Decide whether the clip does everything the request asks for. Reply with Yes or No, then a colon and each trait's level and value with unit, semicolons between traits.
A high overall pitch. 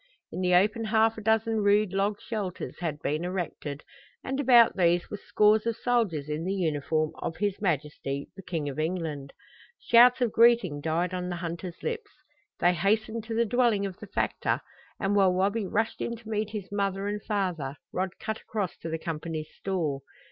Yes: high, 195 Hz